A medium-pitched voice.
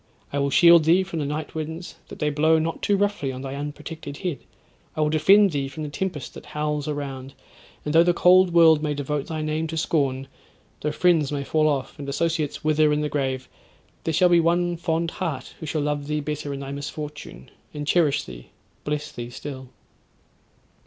Yes: medium, 150 Hz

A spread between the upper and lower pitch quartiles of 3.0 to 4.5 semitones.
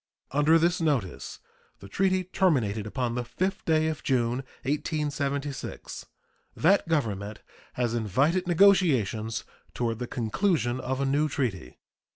No: wide, 5.6 semitones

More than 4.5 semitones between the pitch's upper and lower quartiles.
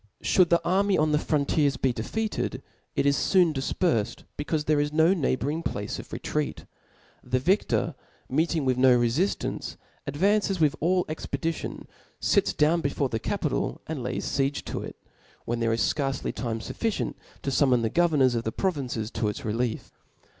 Yes: average, 4.9 semitones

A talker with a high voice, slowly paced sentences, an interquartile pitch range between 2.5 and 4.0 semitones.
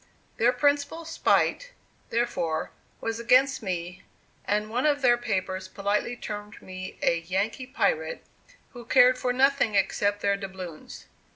No: high, 220 Hz; slow, 130 wpm; average, 5.0 semitones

